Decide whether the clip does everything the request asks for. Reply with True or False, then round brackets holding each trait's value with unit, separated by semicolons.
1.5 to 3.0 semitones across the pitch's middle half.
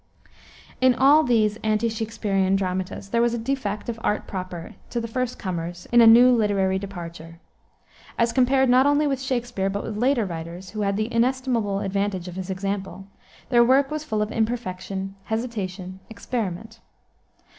False (4.1 semitones)